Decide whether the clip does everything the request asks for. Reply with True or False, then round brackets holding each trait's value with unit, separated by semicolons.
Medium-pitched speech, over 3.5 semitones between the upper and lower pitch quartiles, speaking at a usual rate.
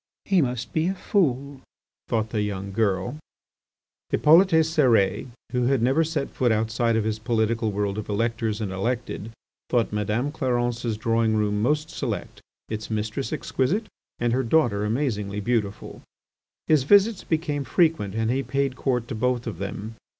False (120 Hz; 4.3 semitones; 150 wpm)